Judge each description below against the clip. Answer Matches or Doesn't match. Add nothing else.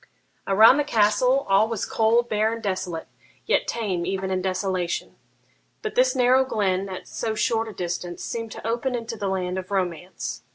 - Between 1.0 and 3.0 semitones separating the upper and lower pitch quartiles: Doesn't match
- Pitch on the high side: Matches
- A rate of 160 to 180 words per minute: Matches